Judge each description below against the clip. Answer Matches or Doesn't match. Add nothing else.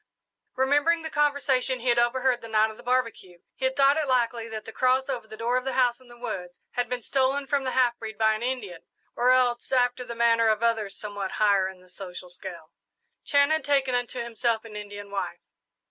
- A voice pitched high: Matches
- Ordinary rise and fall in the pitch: Matches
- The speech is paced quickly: Matches